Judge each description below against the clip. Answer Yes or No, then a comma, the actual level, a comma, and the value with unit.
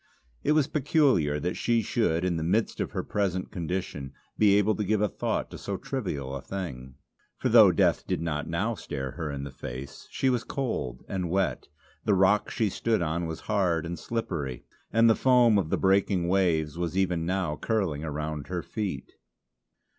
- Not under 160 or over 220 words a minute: Yes, average, 190 wpm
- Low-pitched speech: Yes, very low, 90 Hz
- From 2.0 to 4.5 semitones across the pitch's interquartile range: No, average, 5.3 semitones